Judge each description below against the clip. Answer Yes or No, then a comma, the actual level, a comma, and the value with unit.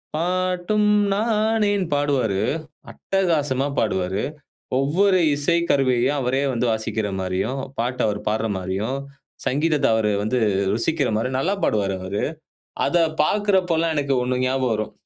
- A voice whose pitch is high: No, low, 135 Hz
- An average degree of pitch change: No, wide, 7.5 semitones